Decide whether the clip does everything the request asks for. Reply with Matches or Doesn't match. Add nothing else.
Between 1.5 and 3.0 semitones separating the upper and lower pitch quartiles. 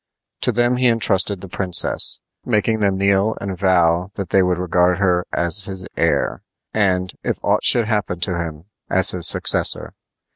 Matches